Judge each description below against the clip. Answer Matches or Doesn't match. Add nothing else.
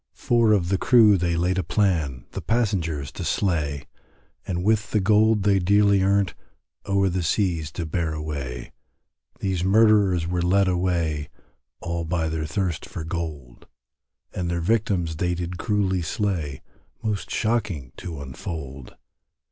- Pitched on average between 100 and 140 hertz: Doesn't match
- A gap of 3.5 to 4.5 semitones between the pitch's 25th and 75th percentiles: Matches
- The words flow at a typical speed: Matches